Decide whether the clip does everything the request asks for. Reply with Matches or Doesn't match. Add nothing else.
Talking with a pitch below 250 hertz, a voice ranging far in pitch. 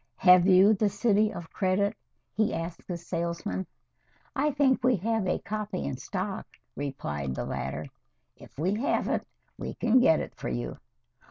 Doesn't match